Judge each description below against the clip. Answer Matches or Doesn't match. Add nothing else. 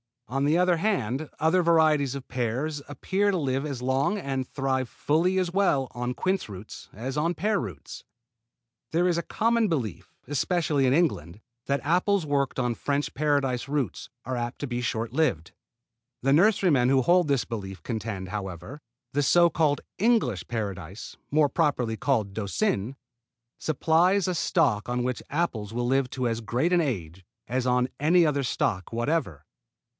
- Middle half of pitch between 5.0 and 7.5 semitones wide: Matches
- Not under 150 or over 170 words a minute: Matches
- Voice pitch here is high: Doesn't match